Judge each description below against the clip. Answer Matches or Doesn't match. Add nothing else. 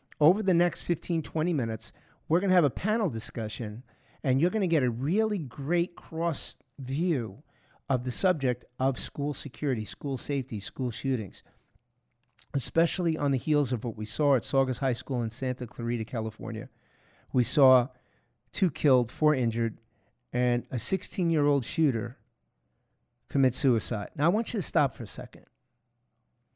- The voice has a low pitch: Matches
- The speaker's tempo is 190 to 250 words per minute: Doesn't match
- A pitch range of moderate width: Matches